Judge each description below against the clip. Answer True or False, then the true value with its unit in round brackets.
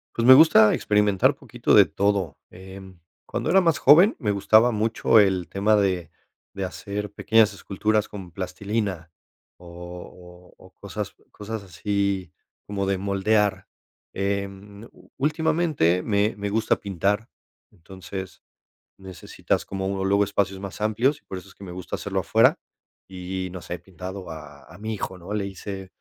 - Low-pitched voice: True (100 Hz)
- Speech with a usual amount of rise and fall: False (2.2 semitones)